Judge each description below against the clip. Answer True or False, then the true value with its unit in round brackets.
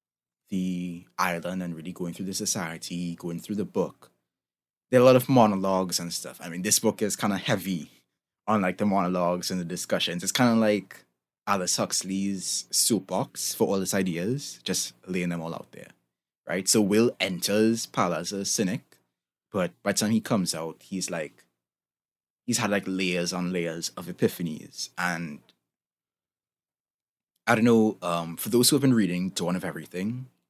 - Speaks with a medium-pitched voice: False (90 Hz)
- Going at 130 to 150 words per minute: False (180 wpm)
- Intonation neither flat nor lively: True (3.3 semitones)